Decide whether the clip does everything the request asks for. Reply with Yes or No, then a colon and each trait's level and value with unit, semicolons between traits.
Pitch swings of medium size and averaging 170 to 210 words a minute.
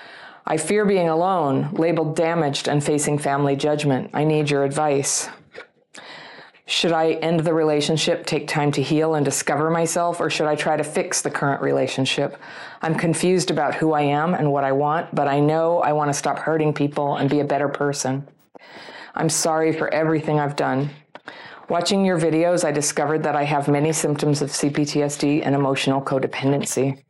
No: narrow, 2.1 semitones; average, 175 wpm